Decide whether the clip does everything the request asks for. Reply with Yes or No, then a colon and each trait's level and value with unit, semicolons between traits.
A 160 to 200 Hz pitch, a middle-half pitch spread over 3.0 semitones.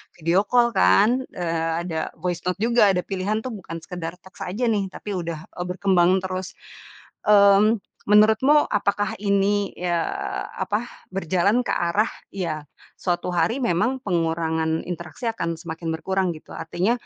Yes: medium, 185 Hz; average, 3.7 semitones